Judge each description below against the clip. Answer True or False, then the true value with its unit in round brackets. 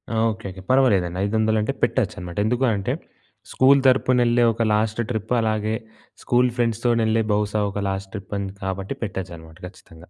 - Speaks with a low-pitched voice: True (110 Hz)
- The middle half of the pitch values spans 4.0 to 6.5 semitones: False (3.4 semitones)